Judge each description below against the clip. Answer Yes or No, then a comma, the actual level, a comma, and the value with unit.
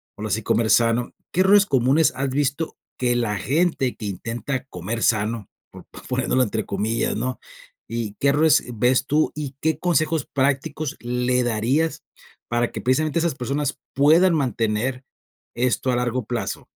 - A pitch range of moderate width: Yes, average, 4.1 semitones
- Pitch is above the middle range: No, low, 125 Hz